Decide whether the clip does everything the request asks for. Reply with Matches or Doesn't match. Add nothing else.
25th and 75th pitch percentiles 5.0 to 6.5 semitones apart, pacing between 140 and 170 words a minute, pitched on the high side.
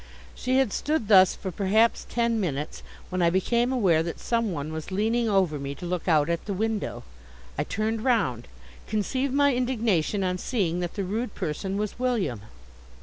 Doesn't match